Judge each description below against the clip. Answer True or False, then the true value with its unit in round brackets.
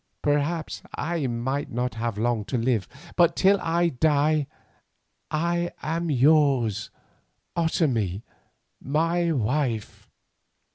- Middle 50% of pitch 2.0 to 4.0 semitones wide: False (5.6 semitones)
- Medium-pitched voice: True (145 Hz)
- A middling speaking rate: False (95 wpm)